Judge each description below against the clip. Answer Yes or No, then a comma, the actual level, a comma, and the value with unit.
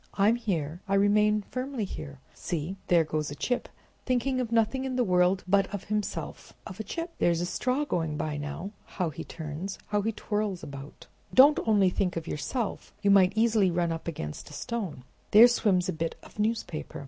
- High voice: Yes, high, 195 Hz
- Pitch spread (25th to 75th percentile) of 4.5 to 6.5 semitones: Yes, average, 5.2 semitones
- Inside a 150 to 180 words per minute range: No, average, 190 wpm